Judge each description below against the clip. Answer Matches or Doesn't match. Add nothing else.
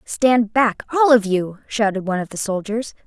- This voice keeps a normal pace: Matches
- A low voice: Doesn't match